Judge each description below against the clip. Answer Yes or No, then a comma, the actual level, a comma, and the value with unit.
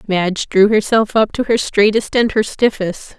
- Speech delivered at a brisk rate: No, average, 190 wpm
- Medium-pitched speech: No, high, 210 Hz